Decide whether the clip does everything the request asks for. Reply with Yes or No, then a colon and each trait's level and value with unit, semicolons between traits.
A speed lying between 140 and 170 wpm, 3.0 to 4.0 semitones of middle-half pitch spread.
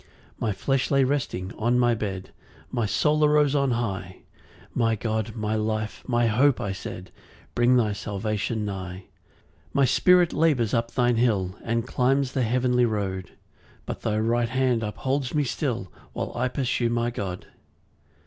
Yes: average, 160 wpm; average, 3.3 semitones